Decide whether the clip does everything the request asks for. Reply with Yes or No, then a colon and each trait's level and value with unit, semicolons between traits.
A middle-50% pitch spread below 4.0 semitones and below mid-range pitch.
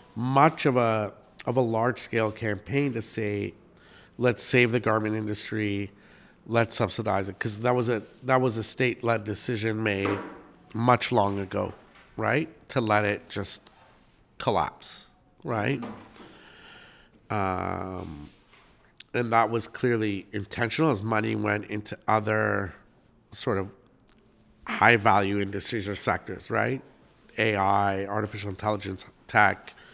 Yes: average, 3.1 semitones; low, 110 Hz